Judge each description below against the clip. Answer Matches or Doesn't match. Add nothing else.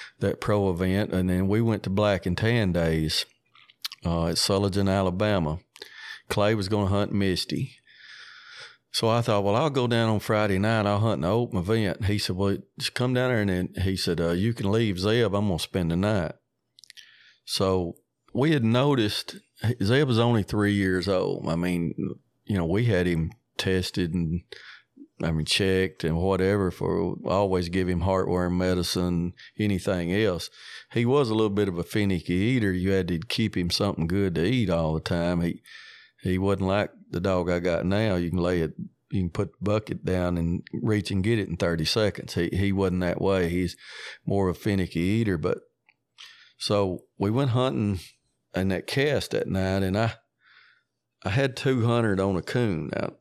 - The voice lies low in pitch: Matches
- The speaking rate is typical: Matches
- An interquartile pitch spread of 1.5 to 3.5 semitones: Matches